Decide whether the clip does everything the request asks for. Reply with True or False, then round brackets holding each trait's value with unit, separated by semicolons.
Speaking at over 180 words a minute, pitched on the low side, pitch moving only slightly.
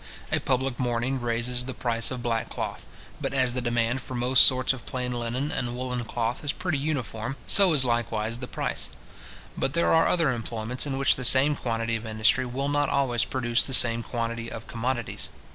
True (195 wpm; 125 Hz; 2.2 semitones)